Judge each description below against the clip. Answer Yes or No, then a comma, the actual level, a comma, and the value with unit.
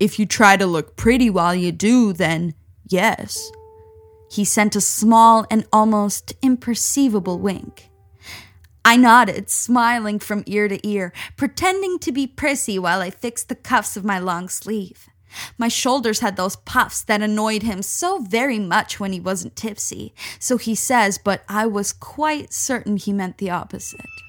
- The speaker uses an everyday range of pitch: Yes, average, 4.1 semitones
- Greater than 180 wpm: No, average, 165 wpm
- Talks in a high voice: Yes, high, 210 Hz